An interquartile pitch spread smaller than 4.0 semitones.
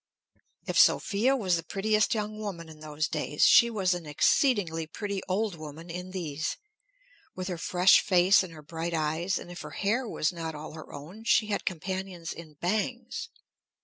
No: average, 4.3 semitones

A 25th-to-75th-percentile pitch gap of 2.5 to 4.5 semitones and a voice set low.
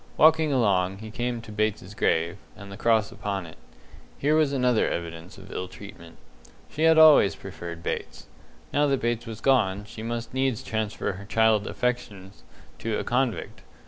Yes: average, 4.2 semitones; low, 110 Hz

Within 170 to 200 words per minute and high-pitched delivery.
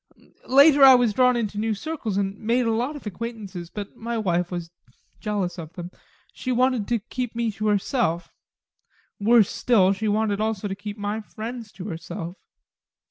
Yes: average, 175 wpm; high, 215 Hz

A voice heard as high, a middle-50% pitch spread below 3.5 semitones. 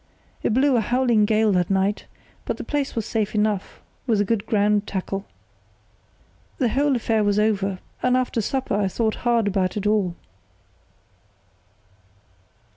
Yes: high, 215 Hz; average, 2.8 semitones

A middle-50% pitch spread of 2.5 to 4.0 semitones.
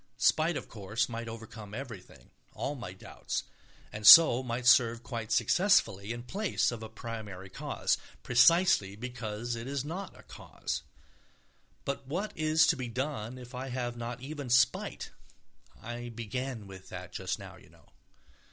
Yes: average, 3.4 semitones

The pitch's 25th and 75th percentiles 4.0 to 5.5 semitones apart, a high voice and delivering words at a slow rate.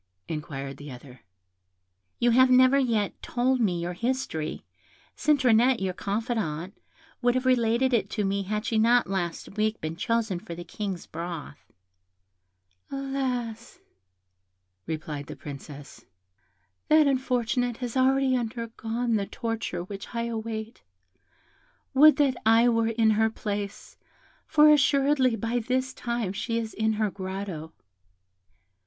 Yes: average, 4.4 semitones; high, 225 Hz; slow, 130 wpm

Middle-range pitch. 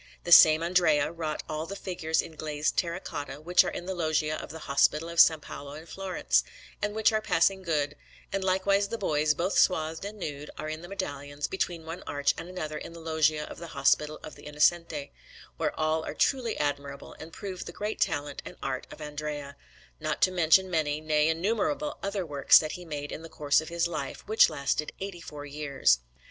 Yes: medium, 160 Hz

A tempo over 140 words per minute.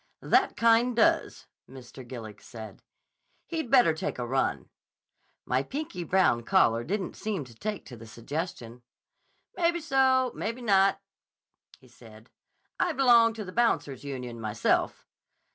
No: slow, 135 wpm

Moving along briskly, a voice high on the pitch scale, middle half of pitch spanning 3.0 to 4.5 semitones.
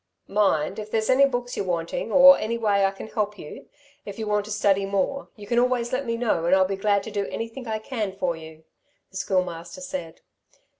Yes: fast, 220 wpm; high, 205 Hz; average, 3.5 semitones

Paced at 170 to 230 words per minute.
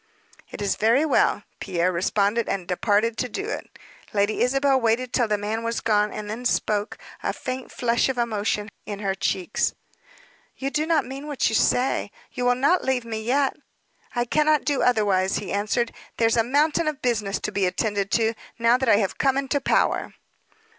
Yes: average, 190 wpm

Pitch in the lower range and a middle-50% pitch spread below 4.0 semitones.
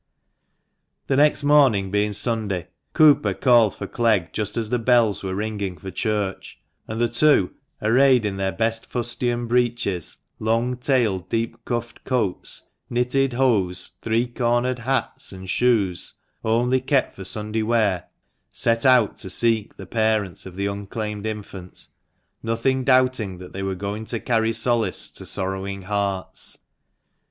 Yes: low, 110 Hz; average, 3.6 semitones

